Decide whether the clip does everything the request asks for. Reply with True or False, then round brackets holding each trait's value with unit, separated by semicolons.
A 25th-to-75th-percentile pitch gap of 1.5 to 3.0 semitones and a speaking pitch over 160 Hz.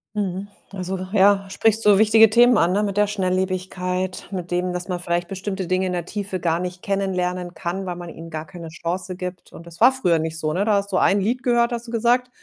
True (2.5 semitones; 185 Hz)